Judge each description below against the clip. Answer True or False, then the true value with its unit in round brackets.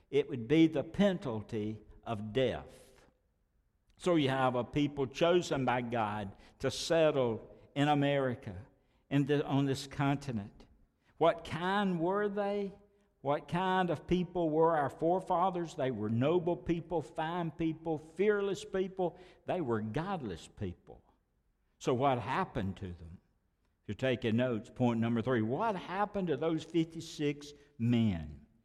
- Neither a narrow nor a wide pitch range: False (6.8 semitones)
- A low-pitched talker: False (145 Hz)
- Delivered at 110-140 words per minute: True (135 wpm)